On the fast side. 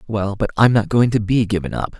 Yes: fast, 270 wpm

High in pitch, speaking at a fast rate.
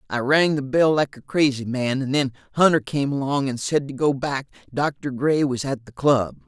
No: low, 135 Hz; fast, 220 wpm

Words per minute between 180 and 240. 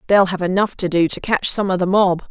No: fast, 285 wpm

